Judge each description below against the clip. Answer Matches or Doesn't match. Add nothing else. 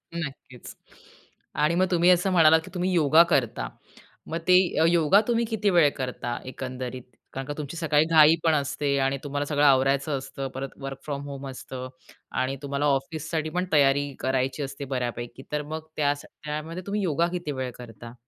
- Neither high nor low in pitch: Matches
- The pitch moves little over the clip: Doesn't match